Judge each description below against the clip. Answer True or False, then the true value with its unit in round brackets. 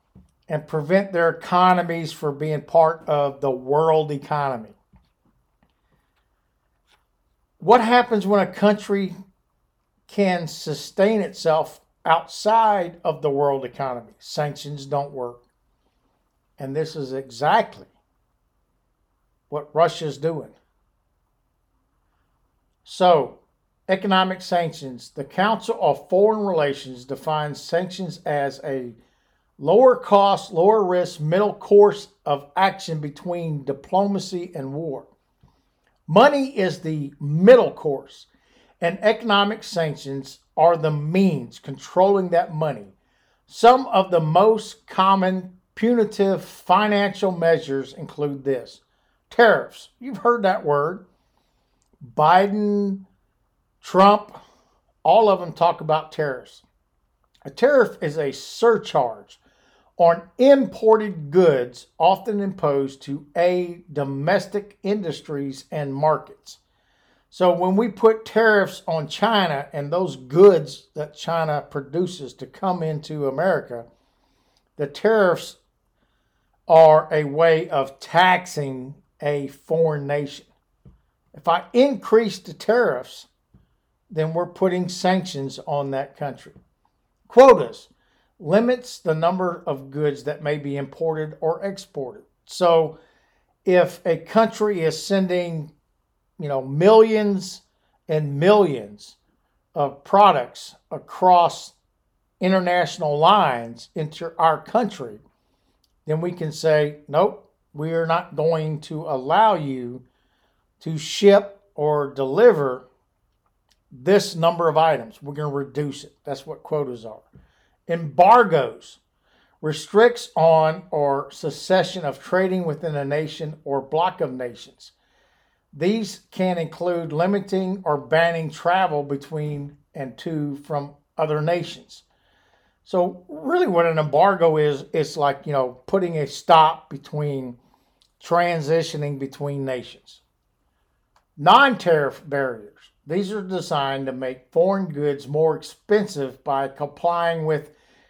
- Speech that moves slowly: True (110 wpm)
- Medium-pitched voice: True (160 Hz)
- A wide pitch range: False (4.8 semitones)